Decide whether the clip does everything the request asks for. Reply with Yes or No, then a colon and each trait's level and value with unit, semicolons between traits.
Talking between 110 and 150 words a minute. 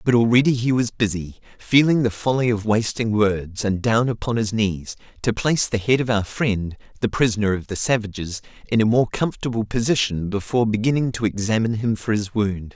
No: average, 195 wpm